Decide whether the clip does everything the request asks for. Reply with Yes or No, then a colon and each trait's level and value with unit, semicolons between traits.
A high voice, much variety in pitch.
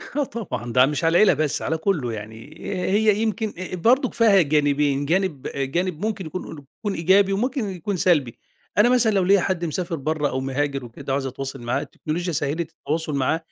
No: medium, 165 Hz; wide, 5.9 semitones